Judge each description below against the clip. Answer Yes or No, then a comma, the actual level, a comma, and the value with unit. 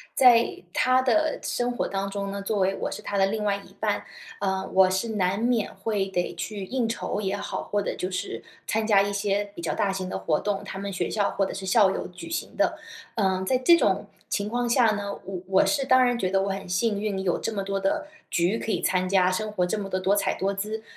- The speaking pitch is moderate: No, high, 200 Hz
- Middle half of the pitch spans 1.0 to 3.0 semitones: Yes, narrow, 2.4 semitones